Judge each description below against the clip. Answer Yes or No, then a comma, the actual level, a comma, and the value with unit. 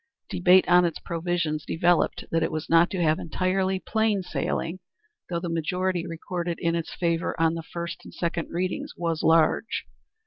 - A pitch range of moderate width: No, narrow, 1.6 semitones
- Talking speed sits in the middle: Yes, average, 170 wpm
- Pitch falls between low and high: Yes, medium, 170 Hz